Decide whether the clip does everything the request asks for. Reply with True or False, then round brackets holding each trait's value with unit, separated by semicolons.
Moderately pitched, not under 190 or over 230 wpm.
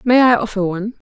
False (220 Hz; 225 wpm)